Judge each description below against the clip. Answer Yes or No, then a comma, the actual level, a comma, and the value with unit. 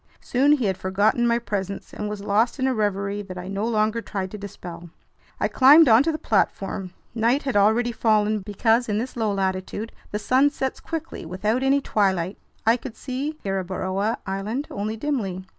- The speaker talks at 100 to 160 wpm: No, average, 180 wpm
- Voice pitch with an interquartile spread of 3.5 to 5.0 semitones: Yes, average, 3.9 semitones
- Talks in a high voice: Yes, high, 215 Hz